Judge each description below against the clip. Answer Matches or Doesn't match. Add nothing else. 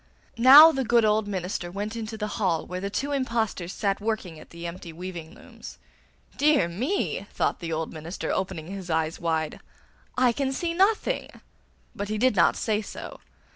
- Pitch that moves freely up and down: Matches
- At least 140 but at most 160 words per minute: Doesn't match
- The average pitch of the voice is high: Matches